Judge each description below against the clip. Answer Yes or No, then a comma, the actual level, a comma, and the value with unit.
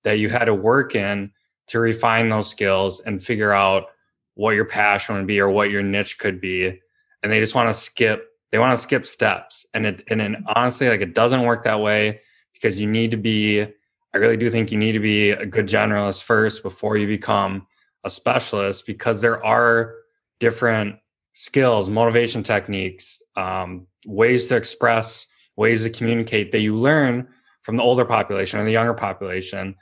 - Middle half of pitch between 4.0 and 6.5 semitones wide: No, narrow, 2.4 semitones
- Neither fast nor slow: Yes, average, 185 wpm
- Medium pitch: No, low, 110 Hz